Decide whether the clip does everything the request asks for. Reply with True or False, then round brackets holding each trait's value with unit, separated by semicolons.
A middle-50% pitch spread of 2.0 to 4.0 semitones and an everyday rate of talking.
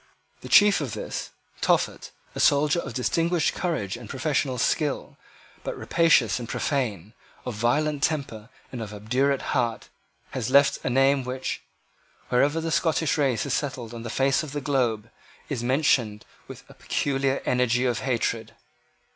True (3.5 semitones; 155 wpm)